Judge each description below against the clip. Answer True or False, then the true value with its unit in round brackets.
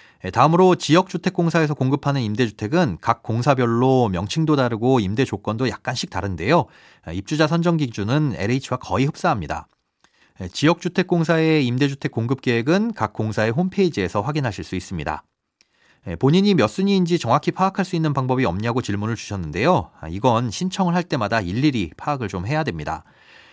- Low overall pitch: True (130 Hz)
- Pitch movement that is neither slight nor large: False (7.2 semitones)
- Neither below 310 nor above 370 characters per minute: False (380 characters per minute)